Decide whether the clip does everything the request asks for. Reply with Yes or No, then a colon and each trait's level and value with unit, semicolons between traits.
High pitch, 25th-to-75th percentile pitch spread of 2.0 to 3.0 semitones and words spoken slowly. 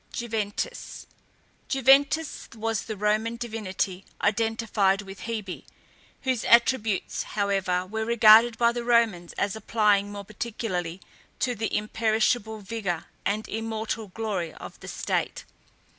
Yes: high, 220 Hz; narrow, 2.4 semitones; slow, 115 wpm